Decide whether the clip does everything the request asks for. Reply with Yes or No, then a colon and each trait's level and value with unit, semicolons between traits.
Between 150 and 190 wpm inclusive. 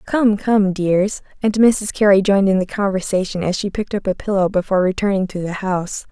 No: fast, 205 wpm